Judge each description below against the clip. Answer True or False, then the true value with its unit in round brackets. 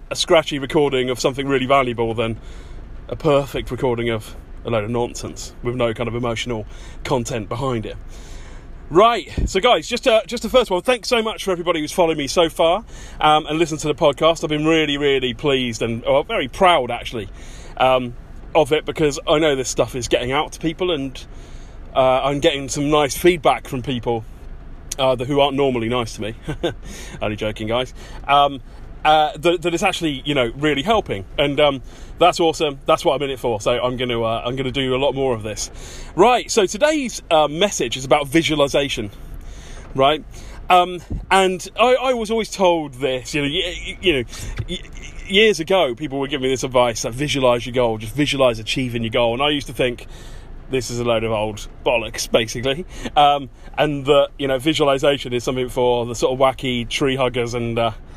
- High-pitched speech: False (135 Hz)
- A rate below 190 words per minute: False (200 wpm)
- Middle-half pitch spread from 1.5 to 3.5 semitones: False (4.6 semitones)